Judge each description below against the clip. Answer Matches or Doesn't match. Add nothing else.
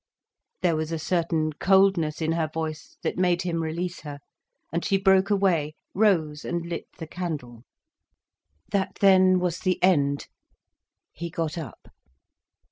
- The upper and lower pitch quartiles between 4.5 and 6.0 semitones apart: Doesn't match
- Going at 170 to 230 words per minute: Doesn't match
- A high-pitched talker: Doesn't match